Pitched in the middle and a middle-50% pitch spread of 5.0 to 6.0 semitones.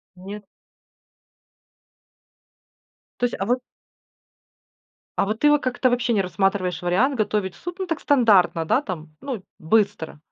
No: high, 210 Hz; average, 5.3 semitones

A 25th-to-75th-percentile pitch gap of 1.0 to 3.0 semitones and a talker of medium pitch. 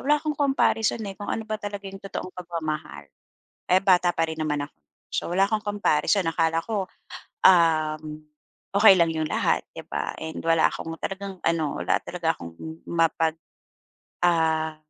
No: average, 3.8 semitones; medium, 170 Hz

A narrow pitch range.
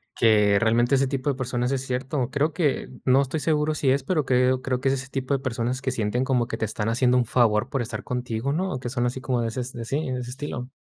Yes: narrow, 2.0 semitones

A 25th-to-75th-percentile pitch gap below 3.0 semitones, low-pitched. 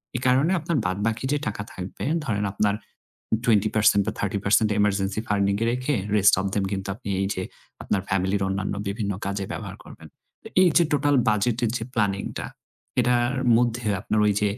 No: average, 3.4 semitones; low, 105 Hz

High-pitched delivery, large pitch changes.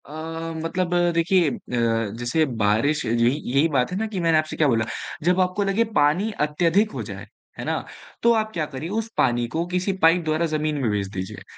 No: medium, 155 Hz; wide, 6.5 semitones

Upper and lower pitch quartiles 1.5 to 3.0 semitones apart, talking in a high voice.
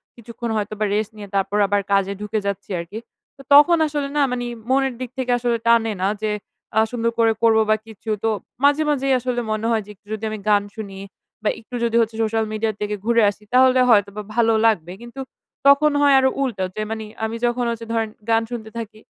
Yes: narrow, 2.6 semitones; high, 225 Hz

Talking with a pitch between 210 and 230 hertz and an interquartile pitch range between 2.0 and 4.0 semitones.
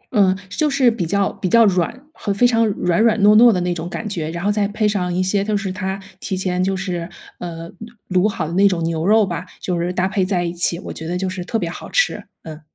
No: high, 190 Hz; average, 3.0 semitones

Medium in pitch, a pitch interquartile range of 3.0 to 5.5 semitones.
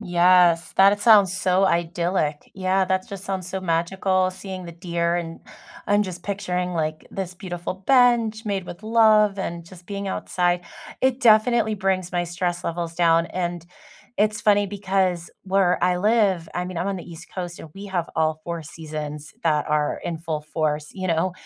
No: medium, 180 Hz; narrow, 2.5 semitones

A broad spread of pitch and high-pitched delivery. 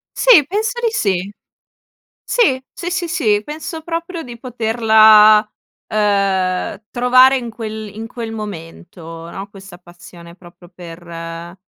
Yes: wide, 6.2 semitones; high, 215 Hz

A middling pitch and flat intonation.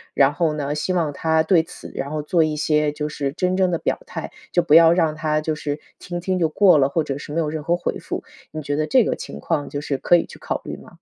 Yes: medium, 155 Hz; narrow, 2.3 semitones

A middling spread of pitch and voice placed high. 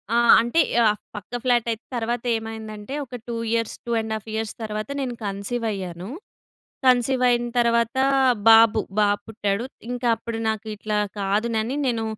No: narrow, 2.0 semitones; high, 225 Hz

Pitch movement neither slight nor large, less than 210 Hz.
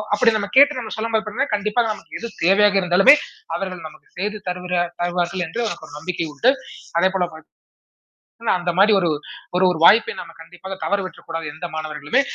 Yes: average, 3.6 semitones; medium, 185 Hz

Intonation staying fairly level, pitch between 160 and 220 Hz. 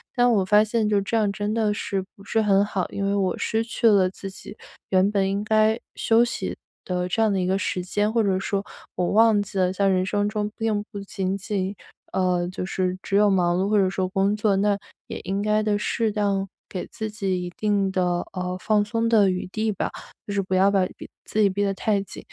Yes: narrow, 2.0 semitones; high, 200 Hz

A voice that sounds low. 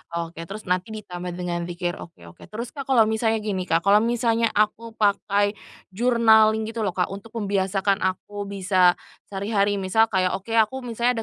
No: high, 205 Hz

